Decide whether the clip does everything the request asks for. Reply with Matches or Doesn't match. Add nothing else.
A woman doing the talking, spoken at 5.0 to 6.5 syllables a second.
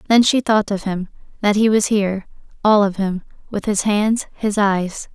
Doesn't match